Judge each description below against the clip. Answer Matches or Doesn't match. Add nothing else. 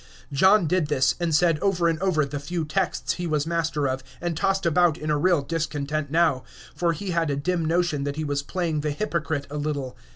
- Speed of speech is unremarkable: Doesn't match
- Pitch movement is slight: Doesn't match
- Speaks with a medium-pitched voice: Matches